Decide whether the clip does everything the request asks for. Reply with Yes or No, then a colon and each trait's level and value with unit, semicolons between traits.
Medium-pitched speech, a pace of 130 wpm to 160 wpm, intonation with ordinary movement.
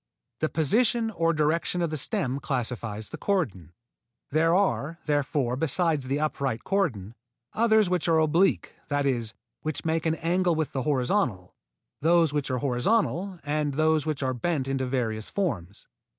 Yes: medium, 150 Hz; average, 155 wpm; average, 4.6 semitones